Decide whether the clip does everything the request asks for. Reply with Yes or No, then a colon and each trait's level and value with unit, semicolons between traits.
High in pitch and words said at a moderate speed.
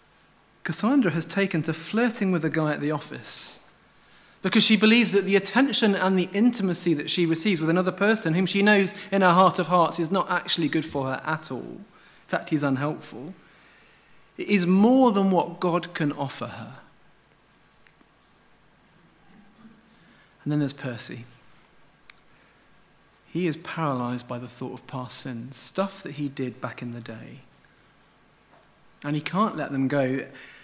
No: medium, 165 Hz; average, 160 wpm